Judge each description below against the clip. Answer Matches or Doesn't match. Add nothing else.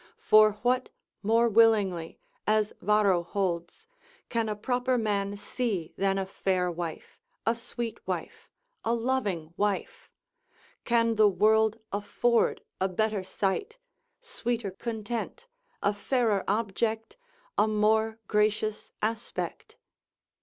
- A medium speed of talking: Doesn't match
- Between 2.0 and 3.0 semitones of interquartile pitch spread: Matches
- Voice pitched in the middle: Doesn't match